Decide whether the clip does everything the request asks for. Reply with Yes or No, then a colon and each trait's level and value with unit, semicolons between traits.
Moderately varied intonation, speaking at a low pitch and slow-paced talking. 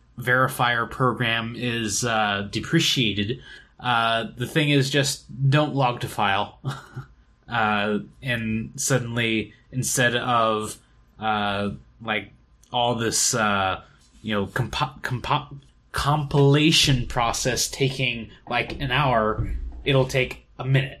Yes: average, 3.5 semitones; low, 120 Hz; slow, 110 wpm